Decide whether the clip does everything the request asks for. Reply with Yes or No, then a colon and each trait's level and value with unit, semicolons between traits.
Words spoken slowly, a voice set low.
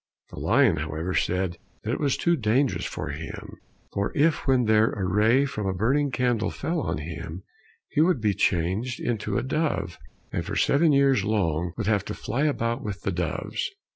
No: average, 190 wpm; low, 110 Hz